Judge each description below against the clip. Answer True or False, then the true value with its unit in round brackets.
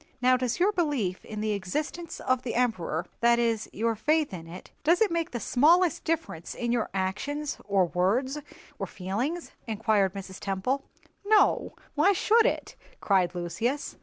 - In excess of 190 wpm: False (155 wpm)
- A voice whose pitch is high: True (235 Hz)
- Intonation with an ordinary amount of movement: False (7.7 semitones)